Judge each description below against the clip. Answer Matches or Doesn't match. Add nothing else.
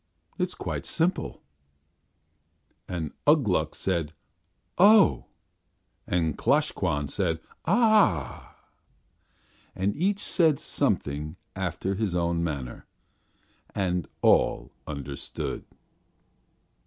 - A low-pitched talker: Matches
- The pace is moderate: Doesn't match